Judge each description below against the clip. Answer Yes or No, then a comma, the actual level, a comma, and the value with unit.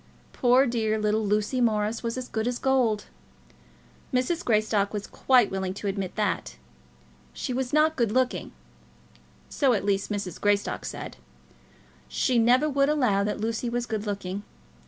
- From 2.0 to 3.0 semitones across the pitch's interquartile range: No, average, 3.5 semitones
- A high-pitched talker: Yes, high, 225 Hz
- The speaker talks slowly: No, average, 155 wpm